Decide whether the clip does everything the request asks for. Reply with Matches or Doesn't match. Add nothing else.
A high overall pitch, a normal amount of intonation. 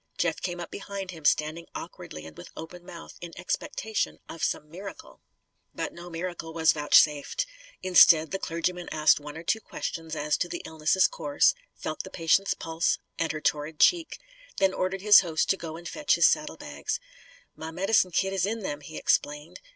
Doesn't match